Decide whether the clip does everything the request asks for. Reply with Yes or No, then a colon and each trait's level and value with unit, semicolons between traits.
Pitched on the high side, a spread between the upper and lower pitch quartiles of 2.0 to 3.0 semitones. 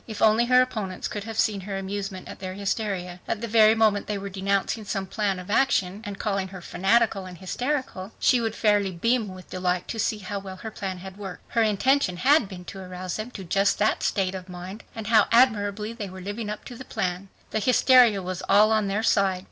Yes: high, 200 Hz; average, 2.7 semitones